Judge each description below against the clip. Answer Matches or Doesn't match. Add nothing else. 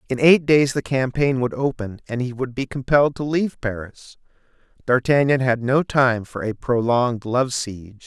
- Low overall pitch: Matches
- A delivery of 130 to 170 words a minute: Doesn't match